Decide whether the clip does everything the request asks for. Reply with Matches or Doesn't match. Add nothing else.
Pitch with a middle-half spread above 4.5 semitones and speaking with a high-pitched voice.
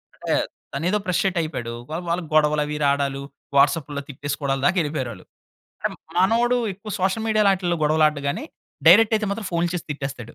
Doesn't match